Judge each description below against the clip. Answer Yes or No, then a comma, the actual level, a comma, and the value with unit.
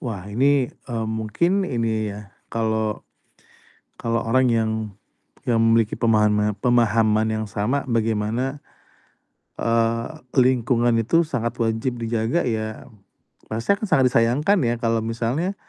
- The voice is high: No, low, 115 Hz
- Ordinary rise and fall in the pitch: No, narrow, 2.2 semitones